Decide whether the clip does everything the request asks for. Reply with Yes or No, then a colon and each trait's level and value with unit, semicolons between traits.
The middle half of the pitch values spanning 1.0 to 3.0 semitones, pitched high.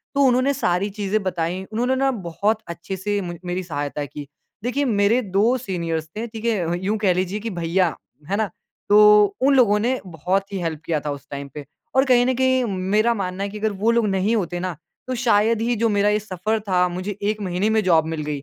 No: average, 4.1 semitones; high, 200 Hz